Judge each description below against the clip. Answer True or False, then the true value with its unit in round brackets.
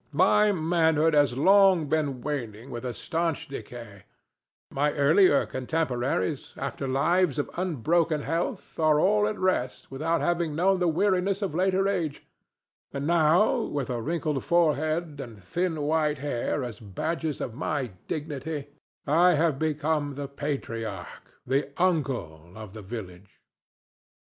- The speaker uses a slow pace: True (130 wpm)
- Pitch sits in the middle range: True (150 Hz)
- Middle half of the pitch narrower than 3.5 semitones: False (4.4 semitones)